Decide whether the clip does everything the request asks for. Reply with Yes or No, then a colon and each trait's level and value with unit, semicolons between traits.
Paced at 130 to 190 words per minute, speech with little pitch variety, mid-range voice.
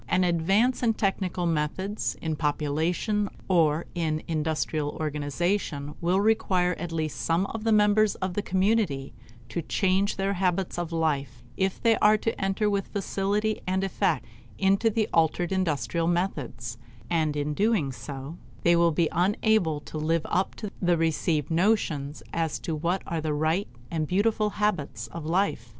No: average, 160 wpm; average, 4.2 semitones; medium, 175 Hz